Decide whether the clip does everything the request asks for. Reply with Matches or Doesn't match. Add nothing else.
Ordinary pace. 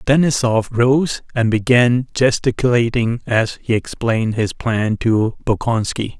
Doesn't match